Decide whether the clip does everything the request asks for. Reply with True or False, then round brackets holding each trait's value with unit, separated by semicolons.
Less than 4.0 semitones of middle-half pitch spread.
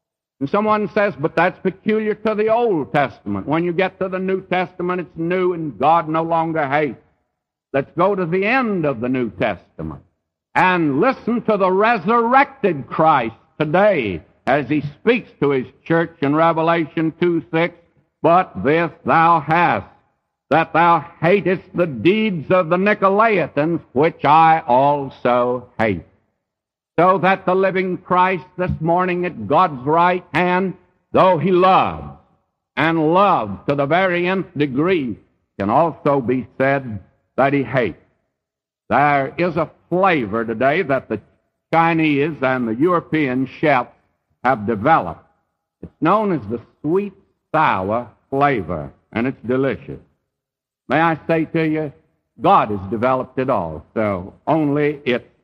False (4.7 semitones)